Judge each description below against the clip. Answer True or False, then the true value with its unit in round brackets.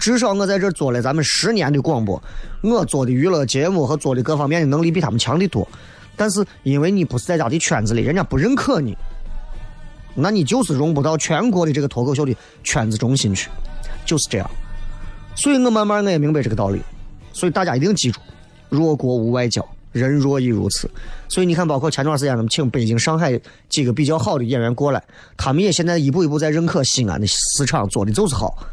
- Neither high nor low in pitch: True (145 Hz)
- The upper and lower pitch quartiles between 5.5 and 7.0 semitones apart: True (6.1 semitones)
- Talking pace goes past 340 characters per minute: False (335 characters per minute)